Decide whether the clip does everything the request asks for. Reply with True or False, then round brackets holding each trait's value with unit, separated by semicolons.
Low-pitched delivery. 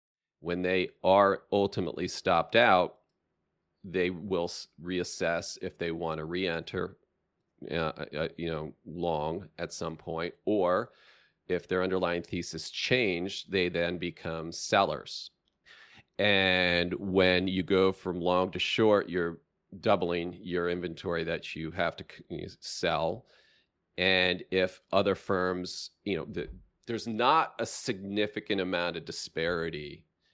True (90 Hz)